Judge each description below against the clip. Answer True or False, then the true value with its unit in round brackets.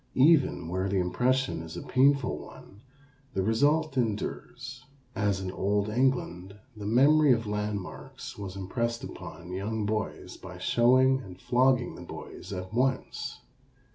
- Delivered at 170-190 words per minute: False (140 wpm)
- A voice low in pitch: True (110 Hz)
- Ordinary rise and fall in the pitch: True (5.0 semitones)